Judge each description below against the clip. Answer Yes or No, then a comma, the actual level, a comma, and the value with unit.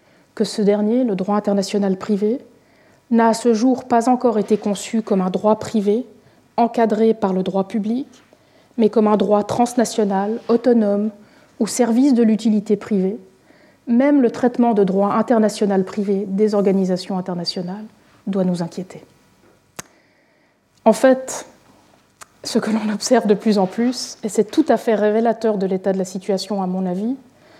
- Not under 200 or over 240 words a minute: No, average, 160 wpm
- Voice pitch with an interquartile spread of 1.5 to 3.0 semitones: Yes, average, 2.7 semitones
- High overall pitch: Yes, high, 215 Hz